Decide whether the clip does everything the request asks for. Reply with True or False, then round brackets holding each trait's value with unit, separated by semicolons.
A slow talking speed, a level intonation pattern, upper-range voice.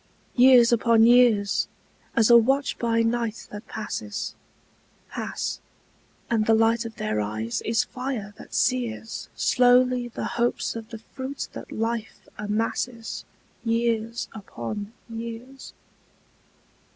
True (115 wpm; 1.8 semitones; 230 Hz)